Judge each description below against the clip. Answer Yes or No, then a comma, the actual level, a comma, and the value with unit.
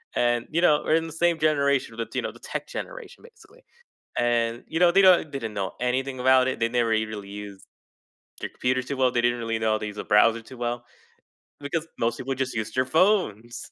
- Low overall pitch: Yes, low, 125 Hz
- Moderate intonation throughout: Yes, average, 4.5 semitones